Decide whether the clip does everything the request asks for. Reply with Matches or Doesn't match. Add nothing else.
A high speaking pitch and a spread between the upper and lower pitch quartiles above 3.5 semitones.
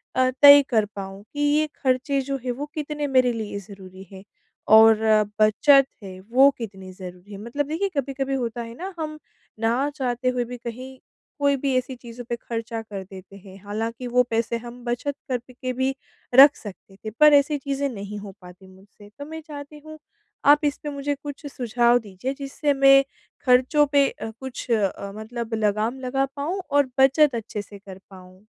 Matches